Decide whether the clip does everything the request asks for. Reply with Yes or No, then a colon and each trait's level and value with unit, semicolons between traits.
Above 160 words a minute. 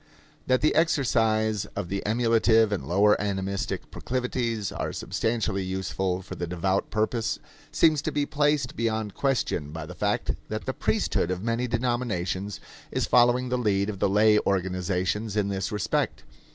No: average, 155 wpm